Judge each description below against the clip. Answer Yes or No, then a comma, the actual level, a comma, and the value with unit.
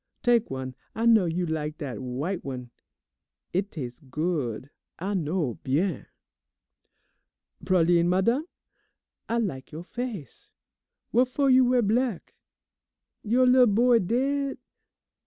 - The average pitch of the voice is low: No, medium, 185 Hz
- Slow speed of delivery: Yes, slow, 120 wpm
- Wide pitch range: Yes, wide, 8.0 semitones